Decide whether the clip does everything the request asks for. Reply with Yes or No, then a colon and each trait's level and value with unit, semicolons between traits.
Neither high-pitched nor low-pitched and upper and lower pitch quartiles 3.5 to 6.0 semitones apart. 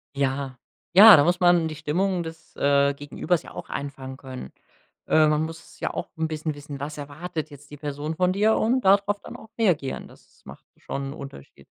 Yes: medium, 155 Hz; average, 4.0 semitones